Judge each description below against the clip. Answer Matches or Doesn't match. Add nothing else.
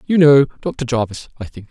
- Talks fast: Matches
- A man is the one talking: Matches